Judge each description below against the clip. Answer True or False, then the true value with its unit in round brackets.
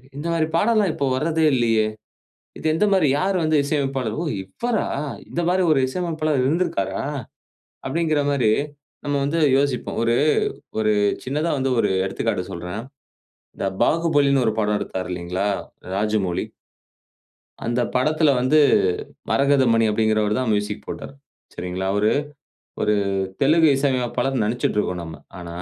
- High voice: False (130 Hz)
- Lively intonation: True (6.6 semitones)